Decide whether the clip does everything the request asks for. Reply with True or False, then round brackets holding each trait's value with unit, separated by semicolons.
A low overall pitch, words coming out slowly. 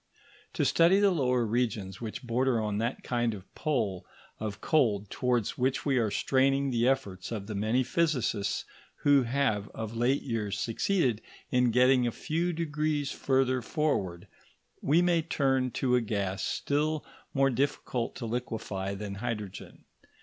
False (125 Hz; 150 wpm)